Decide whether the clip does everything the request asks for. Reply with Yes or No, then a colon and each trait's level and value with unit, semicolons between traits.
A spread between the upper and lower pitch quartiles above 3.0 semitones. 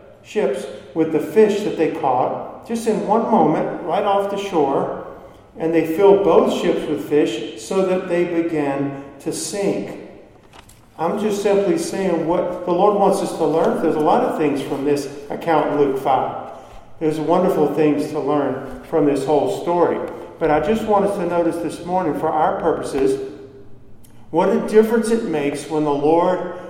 Yes: average, 4.9 semitones